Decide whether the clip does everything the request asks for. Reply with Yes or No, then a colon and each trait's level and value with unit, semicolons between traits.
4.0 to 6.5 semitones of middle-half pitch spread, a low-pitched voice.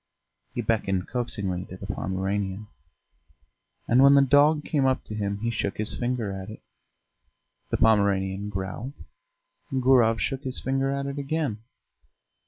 Yes: average, 5.2 semitones; low, 115 Hz